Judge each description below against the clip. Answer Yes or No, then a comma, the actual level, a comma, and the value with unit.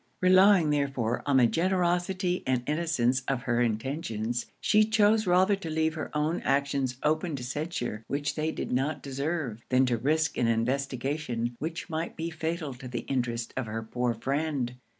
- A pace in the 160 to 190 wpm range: Yes, average, 170 wpm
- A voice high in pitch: No, medium, 140 Hz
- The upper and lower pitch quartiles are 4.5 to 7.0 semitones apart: Yes, average, 5.0 semitones